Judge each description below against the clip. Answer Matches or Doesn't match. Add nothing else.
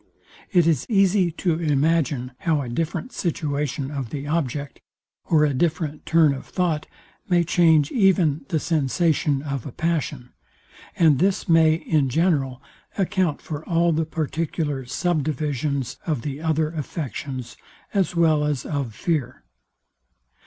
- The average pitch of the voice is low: Doesn't match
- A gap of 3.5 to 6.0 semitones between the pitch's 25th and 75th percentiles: Doesn't match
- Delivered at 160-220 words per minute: Doesn't match